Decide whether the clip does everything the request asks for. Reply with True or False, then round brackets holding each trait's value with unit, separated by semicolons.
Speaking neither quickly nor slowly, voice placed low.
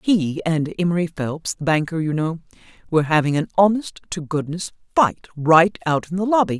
False (180 wpm; 165 Hz)